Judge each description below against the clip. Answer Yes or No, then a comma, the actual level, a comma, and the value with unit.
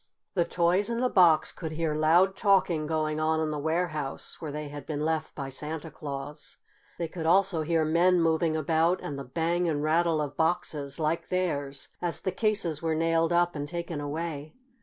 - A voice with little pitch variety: Yes, narrow, 2.1 semitones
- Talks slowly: No, average, 190 wpm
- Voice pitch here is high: No, medium, 160 Hz